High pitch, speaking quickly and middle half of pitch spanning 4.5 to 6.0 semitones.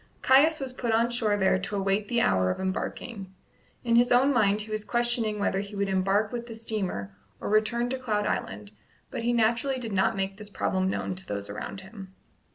No: high, 210 Hz; fast, 210 wpm; average, 3.7 semitones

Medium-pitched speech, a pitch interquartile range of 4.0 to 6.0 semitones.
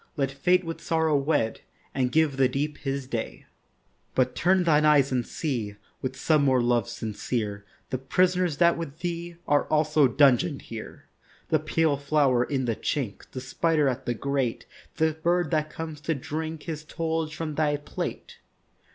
No: medium, 145 Hz; average, 3.6 semitones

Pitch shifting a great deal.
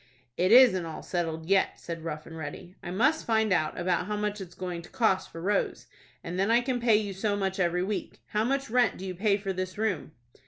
No: average, 3.7 semitones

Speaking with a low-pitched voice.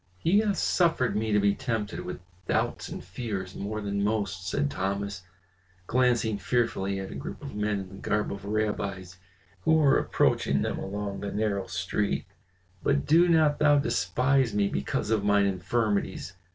Yes: low, 105 Hz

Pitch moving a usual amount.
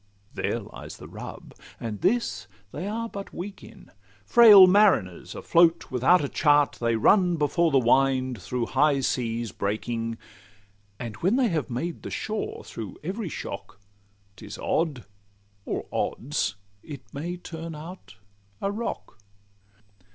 No: wide, 7.4 semitones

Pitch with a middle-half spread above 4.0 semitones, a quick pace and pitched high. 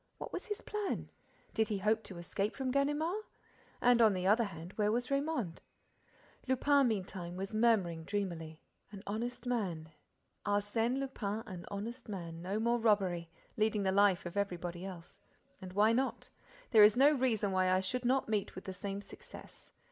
No: average, 4.5 semitones; average, 160 wpm; high, 205 Hz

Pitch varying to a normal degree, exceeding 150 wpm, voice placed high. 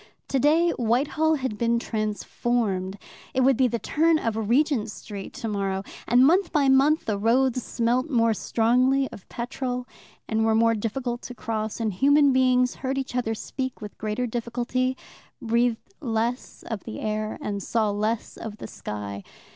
Yes: average, 3.1 semitones; average, 160 wpm; high, 235 Hz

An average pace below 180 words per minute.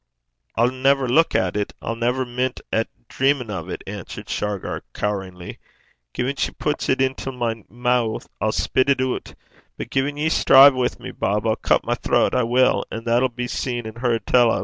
No: average, 195 wpm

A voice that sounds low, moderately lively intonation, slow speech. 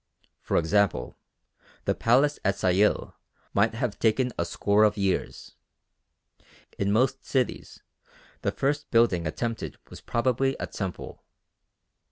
Yes: low, 110 Hz; average, 4.1 semitones; slow, 120 wpm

